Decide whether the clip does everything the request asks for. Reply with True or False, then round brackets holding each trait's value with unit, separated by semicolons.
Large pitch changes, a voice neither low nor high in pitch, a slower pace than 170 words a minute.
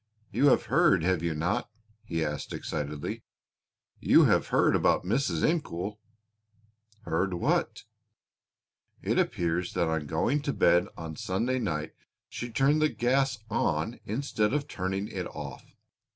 False (7.8 semitones; 95 Hz; 135 wpm)